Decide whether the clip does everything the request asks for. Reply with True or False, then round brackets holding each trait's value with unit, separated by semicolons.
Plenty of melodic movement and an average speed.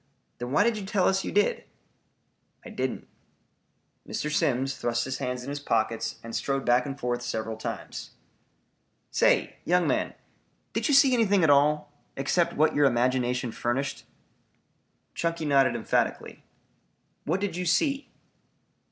True (6.4 semitones; 145 wpm)